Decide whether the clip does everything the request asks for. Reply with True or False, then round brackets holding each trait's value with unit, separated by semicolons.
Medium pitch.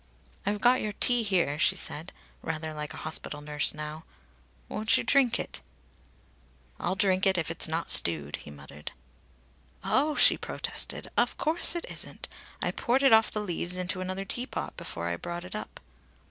True (180 Hz)